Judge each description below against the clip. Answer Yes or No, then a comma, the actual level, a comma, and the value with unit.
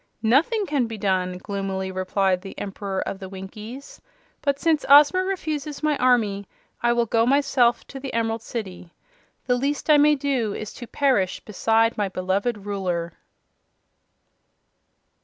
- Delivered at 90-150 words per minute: Yes, average, 145 wpm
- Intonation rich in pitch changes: Yes, wide, 6.1 semitones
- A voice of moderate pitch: No, high, 225 Hz